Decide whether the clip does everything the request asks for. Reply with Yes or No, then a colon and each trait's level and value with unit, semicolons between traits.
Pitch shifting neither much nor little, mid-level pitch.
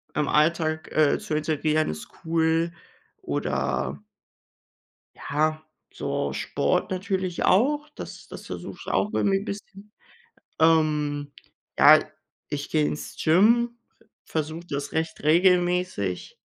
Yes: average, 3.4 semitones; medium, 160 Hz